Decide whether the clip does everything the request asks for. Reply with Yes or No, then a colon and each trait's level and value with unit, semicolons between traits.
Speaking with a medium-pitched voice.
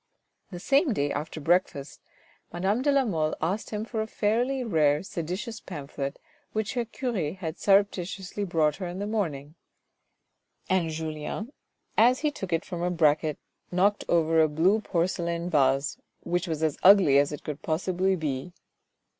Yes: medium, 175 Hz